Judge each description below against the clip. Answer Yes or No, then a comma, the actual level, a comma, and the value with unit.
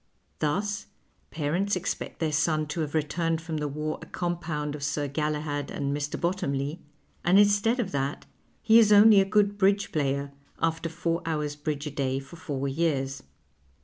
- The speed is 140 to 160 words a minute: No, average, 170 wpm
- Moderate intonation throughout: Yes, average, 3.9 semitones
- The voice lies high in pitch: No, medium, 155 Hz